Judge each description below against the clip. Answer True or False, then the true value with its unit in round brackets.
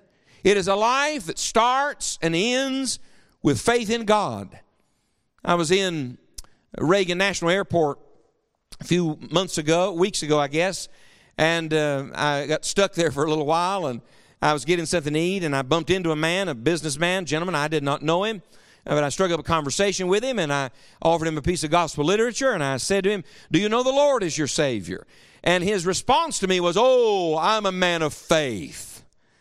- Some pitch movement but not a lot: True (4.2 semitones)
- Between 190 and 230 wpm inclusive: True (205 wpm)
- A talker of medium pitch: True (175 Hz)